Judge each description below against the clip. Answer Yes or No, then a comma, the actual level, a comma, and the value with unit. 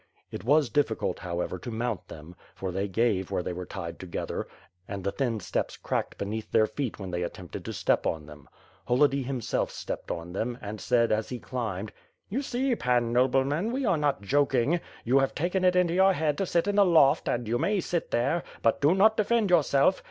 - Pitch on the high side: No, low, 125 Hz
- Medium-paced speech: No, fast, 210 wpm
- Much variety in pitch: Yes, wide, 8.8 semitones